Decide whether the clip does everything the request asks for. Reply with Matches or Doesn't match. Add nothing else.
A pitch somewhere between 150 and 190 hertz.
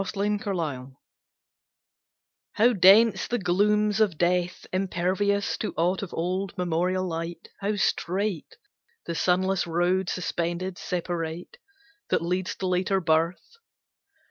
Matches